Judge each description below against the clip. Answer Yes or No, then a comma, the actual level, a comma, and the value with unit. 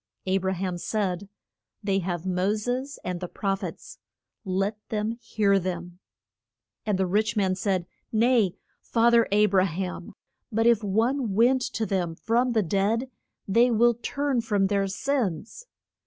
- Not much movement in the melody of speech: No, average, 3.5 semitones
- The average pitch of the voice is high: Yes, high, 205 Hz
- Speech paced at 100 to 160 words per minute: Yes, average, 155 wpm